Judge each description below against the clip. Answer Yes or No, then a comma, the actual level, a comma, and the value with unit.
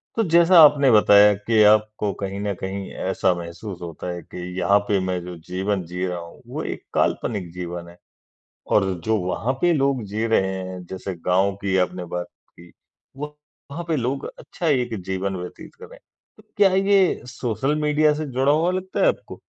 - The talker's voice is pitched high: No, low, 105 Hz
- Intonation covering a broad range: Yes, wide, 7.9 semitones